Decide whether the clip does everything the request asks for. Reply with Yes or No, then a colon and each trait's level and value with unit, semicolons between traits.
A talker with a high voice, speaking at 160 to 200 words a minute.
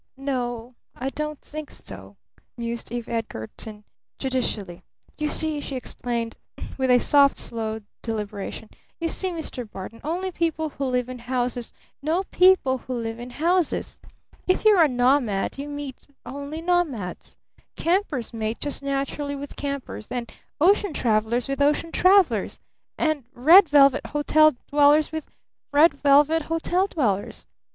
No: very high, 275 Hz; average, 140 wpm